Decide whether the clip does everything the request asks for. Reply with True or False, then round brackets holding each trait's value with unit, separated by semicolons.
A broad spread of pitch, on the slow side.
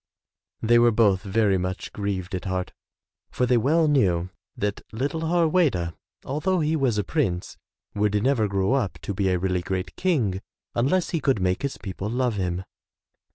False (6.5 semitones; 175 wpm)